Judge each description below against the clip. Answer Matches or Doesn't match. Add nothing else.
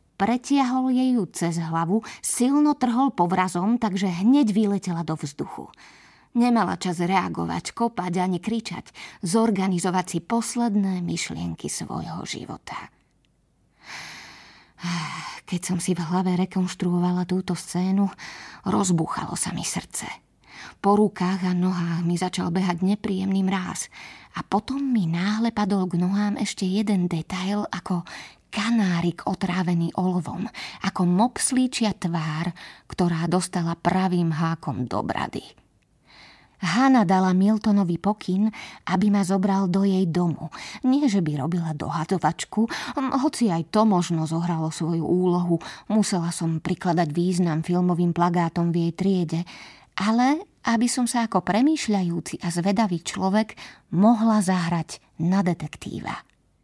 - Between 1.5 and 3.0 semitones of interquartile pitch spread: Doesn't match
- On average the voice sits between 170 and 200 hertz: Matches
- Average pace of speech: Matches